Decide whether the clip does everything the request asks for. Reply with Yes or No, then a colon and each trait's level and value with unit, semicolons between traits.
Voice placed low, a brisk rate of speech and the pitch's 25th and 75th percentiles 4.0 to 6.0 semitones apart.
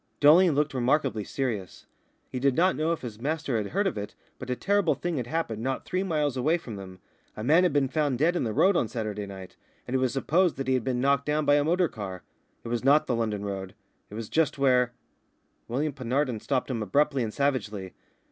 Yes: low, 130 Hz; fast, 230 wpm; average, 5.1 semitones